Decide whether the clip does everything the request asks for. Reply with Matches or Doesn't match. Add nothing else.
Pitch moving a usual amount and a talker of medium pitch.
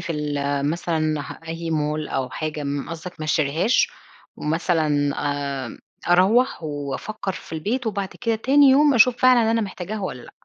Doesn't match